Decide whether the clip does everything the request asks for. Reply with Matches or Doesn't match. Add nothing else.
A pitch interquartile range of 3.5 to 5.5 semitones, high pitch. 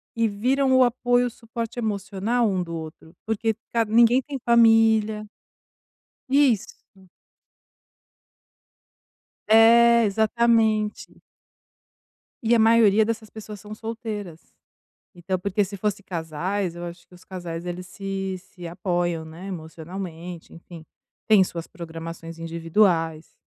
Matches